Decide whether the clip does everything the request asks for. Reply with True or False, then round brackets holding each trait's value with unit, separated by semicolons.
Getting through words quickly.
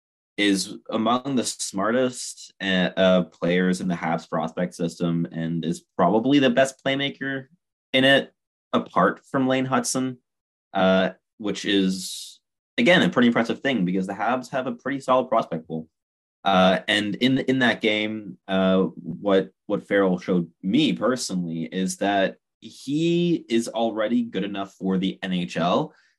False (145 wpm)